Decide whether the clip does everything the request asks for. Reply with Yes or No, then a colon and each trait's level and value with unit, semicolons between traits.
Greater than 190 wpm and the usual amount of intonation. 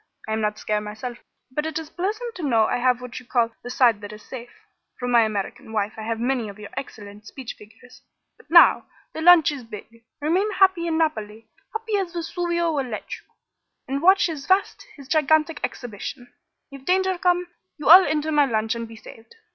No: fast, 205 wpm; wide, 7.0 semitones